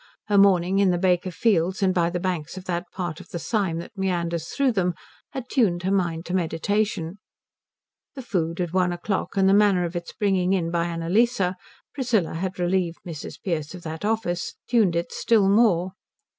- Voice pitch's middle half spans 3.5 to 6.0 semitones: No, average, 2.7 semitones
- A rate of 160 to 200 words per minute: Yes, average, 190 wpm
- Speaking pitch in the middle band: Yes, medium, 180 Hz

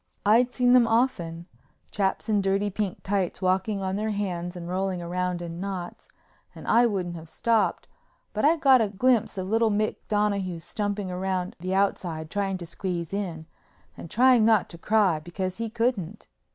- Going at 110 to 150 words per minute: No, average, 165 wpm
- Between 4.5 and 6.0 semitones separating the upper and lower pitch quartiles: No, average, 3.3 semitones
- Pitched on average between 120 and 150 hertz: No, high, 195 Hz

